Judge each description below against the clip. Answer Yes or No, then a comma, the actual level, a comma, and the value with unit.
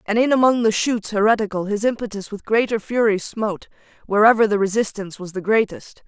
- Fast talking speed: No, average, 180 wpm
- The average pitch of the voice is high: Yes, high, 215 Hz